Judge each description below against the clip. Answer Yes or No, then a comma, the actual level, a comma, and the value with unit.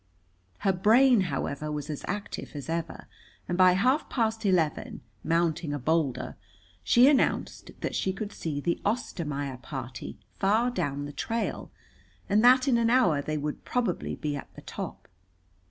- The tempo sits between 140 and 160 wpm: Yes, average, 155 wpm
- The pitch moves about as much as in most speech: No, wide, 7.5 semitones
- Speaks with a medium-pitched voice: Yes, medium, 175 Hz